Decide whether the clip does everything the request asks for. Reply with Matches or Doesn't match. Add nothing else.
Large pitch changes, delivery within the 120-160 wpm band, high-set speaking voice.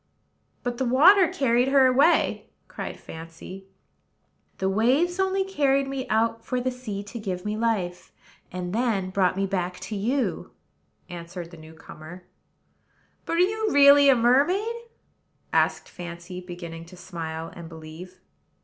Matches